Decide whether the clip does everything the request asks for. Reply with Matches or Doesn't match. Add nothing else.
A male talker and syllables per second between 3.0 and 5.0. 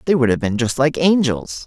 Doesn't match